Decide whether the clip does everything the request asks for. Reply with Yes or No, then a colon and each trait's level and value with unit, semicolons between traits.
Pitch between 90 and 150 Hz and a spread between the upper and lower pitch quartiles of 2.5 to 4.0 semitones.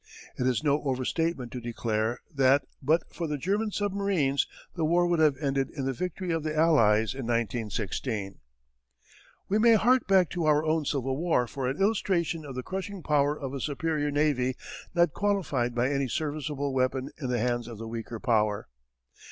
No: medium, 140 Hz; average, 4.8 semitones